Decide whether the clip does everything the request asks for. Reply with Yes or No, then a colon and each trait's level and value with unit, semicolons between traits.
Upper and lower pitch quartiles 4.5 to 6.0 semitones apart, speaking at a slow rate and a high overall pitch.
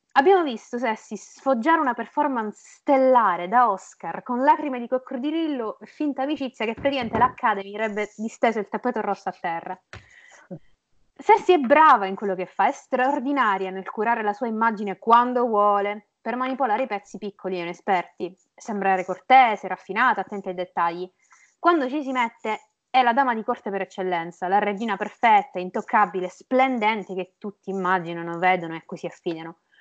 No: average, 5.2 semitones; average, 155 wpm; high, 220 Hz